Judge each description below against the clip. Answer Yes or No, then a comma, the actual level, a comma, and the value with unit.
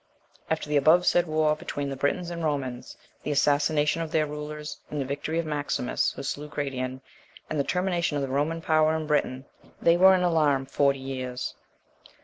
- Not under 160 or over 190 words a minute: Yes, average, 185 wpm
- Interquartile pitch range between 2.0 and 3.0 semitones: Yes, narrow, 2.4 semitones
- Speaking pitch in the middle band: Yes, medium, 150 Hz